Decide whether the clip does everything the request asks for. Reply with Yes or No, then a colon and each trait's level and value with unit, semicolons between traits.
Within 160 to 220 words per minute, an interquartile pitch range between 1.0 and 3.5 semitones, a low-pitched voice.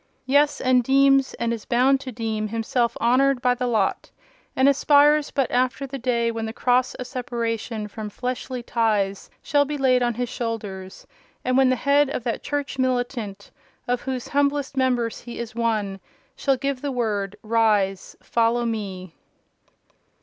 No: average, 165 wpm; average, 2.9 semitones; high, 245 Hz